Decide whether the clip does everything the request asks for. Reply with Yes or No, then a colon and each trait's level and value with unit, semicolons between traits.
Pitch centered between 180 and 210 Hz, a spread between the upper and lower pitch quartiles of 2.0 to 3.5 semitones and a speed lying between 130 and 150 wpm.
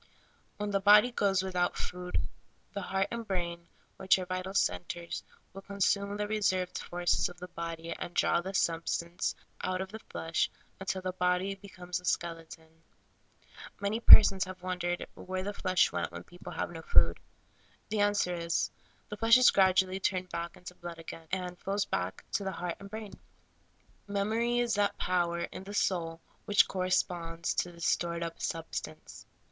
No: medium, 185 Hz; narrow, 2.6 semitones; average, 175 wpm